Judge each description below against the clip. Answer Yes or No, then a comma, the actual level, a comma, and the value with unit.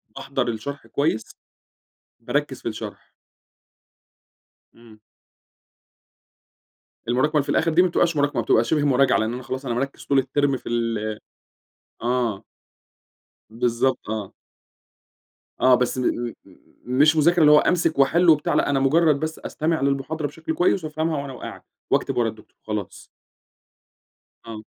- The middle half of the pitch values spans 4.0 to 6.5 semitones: Yes, average, 4.5 semitones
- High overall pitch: No, low, 135 Hz